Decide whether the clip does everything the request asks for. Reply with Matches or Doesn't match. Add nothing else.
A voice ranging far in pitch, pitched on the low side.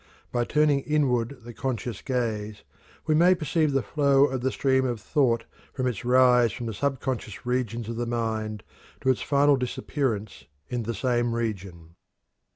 Doesn't match